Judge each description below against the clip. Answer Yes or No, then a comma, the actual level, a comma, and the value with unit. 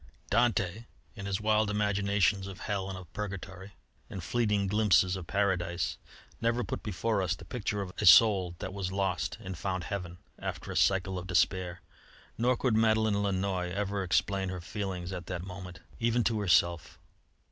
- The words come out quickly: No, average, 170 wpm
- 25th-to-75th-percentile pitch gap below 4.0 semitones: Yes, narrow, 2.4 semitones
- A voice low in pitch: Yes, very low, 95 Hz